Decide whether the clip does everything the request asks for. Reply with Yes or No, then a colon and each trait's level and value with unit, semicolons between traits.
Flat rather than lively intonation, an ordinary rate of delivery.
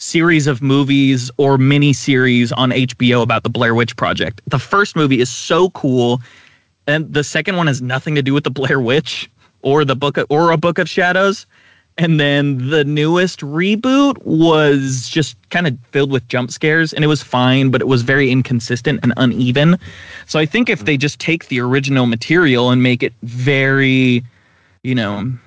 No: average, 3.7 semitones; average, 190 wpm